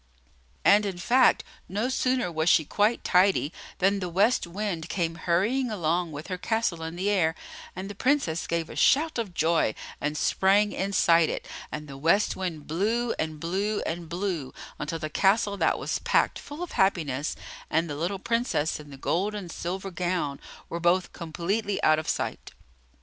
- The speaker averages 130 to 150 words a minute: No, average, 175 wpm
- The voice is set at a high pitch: No, medium, 180 Hz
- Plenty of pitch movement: No, average, 4.0 semitones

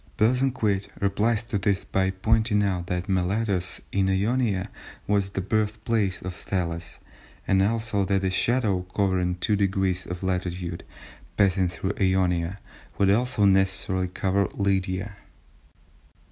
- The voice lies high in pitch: No, very low, 95 Hz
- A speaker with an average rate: No, slow, 125 wpm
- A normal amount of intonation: No, narrow, 2.1 semitones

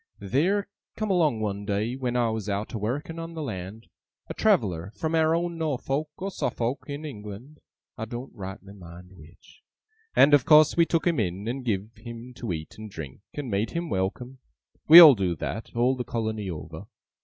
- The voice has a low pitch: Yes, low, 120 Hz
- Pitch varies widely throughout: Yes, wide, 7.1 semitones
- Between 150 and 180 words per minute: No, average, 190 wpm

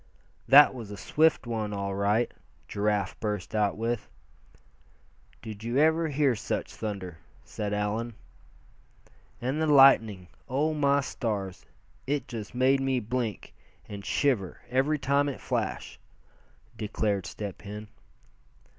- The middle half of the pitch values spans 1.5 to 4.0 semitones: No, average, 4.7 semitones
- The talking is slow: Yes, slow, 125 wpm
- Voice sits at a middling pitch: No, low, 115 Hz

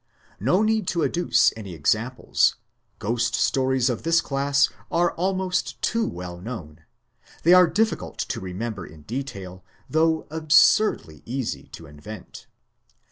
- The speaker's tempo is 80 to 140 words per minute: Yes, slow, 135 wpm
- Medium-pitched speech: No, low, 130 Hz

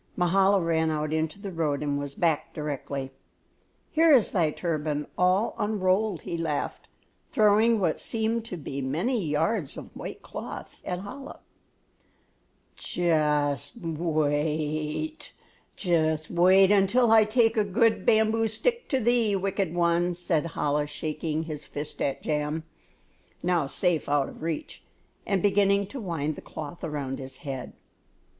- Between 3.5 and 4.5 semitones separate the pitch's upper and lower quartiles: No, average, 5.2 semitones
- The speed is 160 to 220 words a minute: No, slow, 135 wpm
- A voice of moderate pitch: Yes, medium, 170 Hz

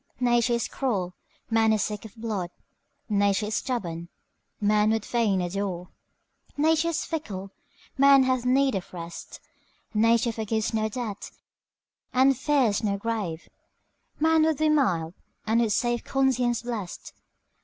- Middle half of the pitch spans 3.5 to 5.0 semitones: Yes, average, 4.3 semitones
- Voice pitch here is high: Yes, high, 225 Hz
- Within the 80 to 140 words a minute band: Yes, slow, 135 wpm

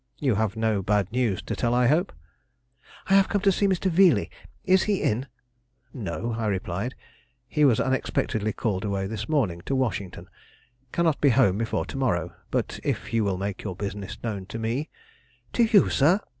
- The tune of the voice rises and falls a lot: Yes, wide, 6.5 semitones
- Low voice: Yes, low, 115 Hz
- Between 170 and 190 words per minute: Yes, average, 185 wpm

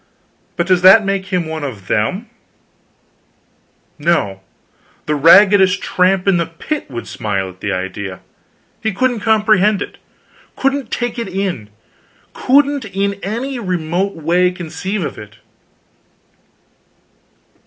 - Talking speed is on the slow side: Yes, slow, 120 wpm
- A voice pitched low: No, medium, 185 Hz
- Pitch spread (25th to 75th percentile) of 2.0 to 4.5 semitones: No, average, 5.2 semitones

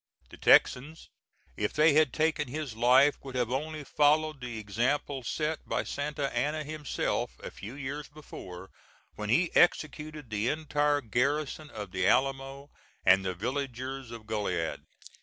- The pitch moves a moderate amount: Yes, average, 4.1 semitones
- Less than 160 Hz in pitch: Yes, low, 135 Hz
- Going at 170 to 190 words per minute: No, average, 145 wpm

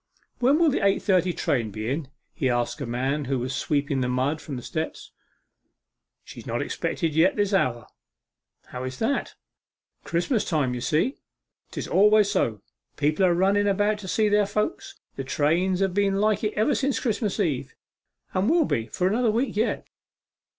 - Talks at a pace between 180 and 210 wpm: Yes, average, 185 wpm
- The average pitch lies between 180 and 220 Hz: Yes, medium, 185 Hz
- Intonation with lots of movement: Yes, wide, 7.5 semitones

